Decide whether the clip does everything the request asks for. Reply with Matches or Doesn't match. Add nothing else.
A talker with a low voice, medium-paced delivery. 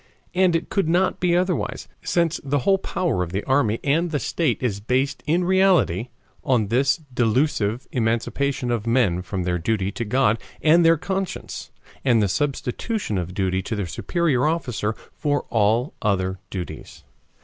Matches